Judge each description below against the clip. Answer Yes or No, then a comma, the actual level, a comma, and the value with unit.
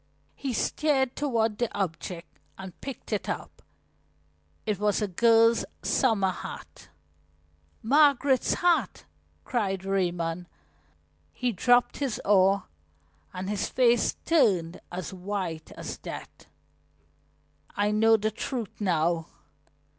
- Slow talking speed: Yes, slow, 110 wpm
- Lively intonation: No, average, 4.6 semitones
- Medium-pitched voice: No, high, 210 Hz